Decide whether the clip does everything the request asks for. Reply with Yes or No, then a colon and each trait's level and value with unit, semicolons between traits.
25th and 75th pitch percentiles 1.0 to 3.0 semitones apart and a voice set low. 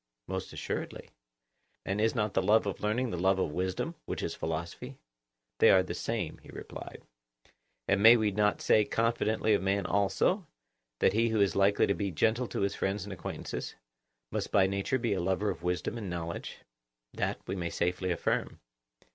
Yes: average, 2.7 semitones; low, 100 Hz